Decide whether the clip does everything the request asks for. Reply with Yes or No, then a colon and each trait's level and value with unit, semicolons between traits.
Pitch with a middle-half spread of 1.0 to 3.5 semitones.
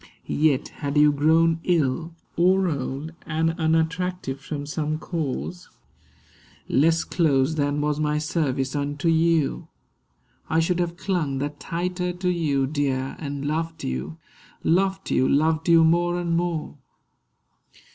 Yes: average, 2.9 semitones